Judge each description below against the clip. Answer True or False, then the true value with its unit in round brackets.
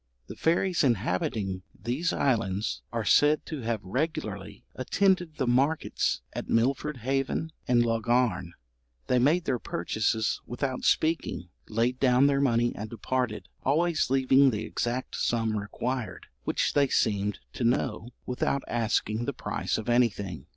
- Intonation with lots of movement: False (3.9 semitones)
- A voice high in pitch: False (125 Hz)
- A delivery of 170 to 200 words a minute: False (135 wpm)